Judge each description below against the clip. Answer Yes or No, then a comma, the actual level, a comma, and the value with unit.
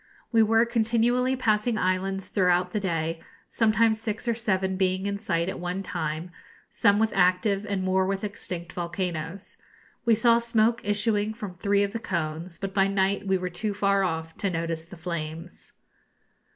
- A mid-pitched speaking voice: No, high, 195 Hz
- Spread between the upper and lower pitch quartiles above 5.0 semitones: No, average, 3.3 semitones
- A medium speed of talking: Yes, average, 170 wpm